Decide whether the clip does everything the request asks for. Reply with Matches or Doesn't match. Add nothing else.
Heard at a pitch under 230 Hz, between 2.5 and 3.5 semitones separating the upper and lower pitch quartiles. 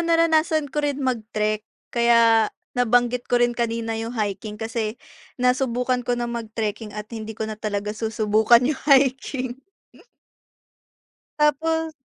Doesn't match